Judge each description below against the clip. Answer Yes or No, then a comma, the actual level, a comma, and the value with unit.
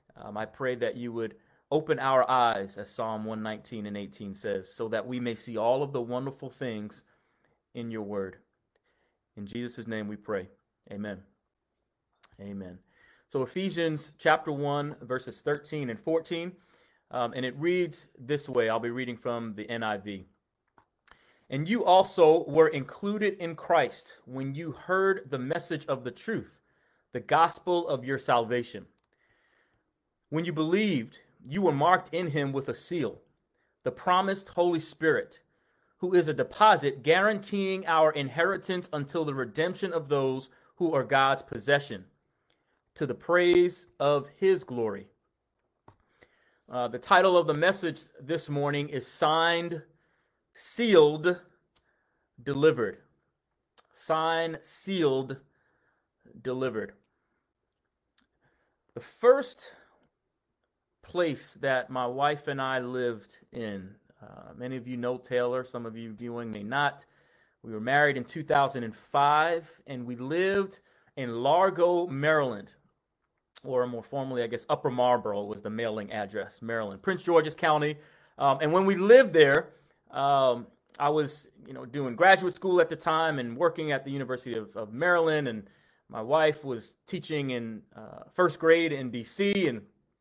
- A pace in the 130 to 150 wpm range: Yes, average, 140 wpm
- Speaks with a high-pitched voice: No, medium, 145 Hz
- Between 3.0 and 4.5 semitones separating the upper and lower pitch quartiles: No, wide, 5.6 semitones